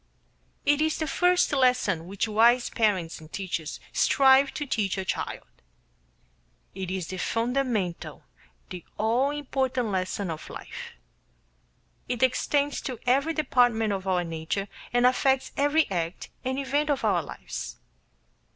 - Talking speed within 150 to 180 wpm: No, slow, 135 wpm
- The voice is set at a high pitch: Yes, high, 245 Hz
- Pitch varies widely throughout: Yes, wide, 6.3 semitones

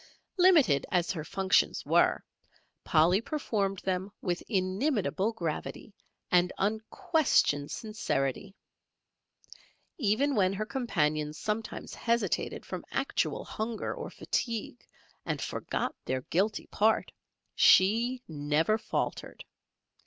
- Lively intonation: No, average, 4.6 semitones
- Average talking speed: No, slow, 100 wpm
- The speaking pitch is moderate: No, high, 200 Hz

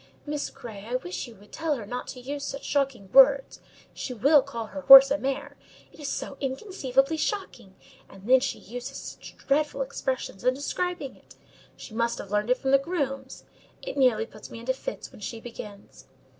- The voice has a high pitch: Yes, very high, 265 Hz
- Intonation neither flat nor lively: Yes, average, 3.2 semitones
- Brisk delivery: No, average, 195 wpm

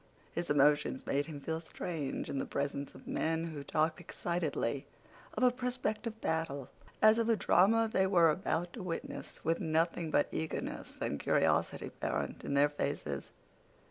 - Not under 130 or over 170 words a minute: Yes, average, 160 wpm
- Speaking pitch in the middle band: Yes, medium, 160 Hz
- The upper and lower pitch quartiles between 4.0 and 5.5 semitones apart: Yes, average, 4.5 semitones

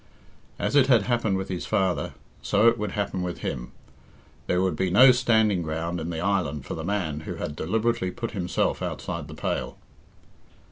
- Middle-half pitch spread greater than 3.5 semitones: Yes, average, 4.5 semitones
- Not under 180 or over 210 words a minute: Yes, average, 185 wpm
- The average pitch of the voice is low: Yes, very low, 95 Hz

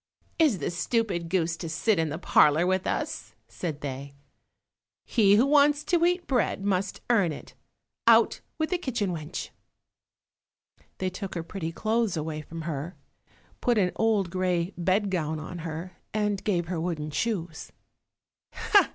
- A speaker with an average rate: Yes, average, 150 wpm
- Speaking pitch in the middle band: Yes, medium, 180 Hz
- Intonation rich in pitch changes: No, average, 4.7 semitones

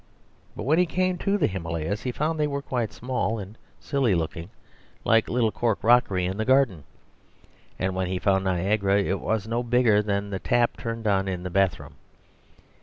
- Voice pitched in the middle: No, low, 105 Hz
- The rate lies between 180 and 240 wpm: Yes, average, 190 wpm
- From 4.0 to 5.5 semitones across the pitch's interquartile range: Yes, average, 4.4 semitones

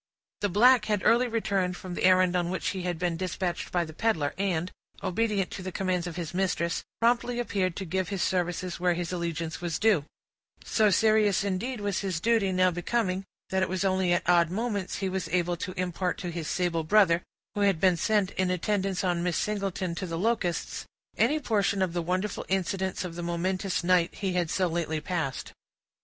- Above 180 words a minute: Yes, average, 200 wpm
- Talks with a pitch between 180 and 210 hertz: Yes, medium, 185 Hz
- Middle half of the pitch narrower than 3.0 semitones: Yes, narrow, 2.4 semitones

